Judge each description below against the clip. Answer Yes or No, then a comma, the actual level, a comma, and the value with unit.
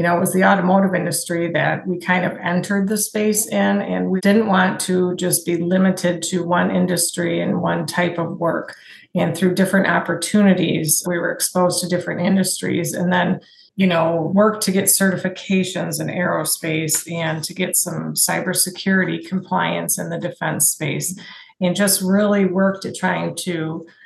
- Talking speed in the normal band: Yes, average, 170 wpm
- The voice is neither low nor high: Yes, medium, 180 Hz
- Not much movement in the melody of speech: Yes, narrow, 1.8 semitones